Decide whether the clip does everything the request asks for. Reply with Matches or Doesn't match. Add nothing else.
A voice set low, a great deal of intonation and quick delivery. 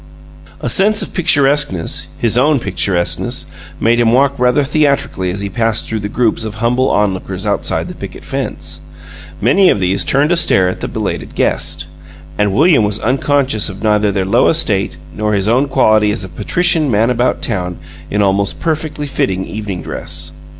Doesn't match